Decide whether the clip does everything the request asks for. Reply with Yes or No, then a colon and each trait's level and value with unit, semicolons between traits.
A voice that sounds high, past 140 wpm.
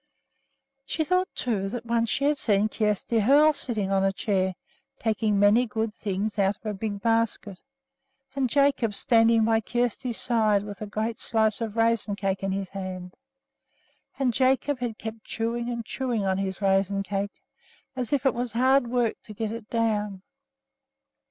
Yes: high, 220 Hz; average, 170 wpm